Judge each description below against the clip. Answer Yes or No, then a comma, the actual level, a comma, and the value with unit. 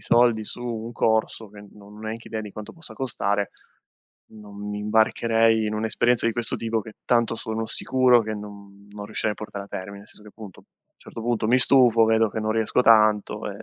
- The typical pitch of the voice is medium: No, low, 110 Hz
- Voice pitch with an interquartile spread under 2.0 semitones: Yes, narrow, 1.6 semitones